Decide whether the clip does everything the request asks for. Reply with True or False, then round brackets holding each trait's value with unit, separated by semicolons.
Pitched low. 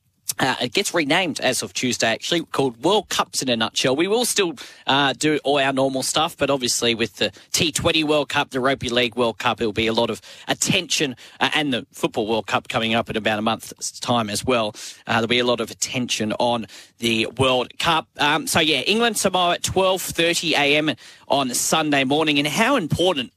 True (130 Hz)